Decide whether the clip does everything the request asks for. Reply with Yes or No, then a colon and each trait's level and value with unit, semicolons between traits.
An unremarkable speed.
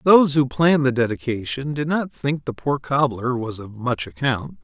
Yes: average, 195 wpm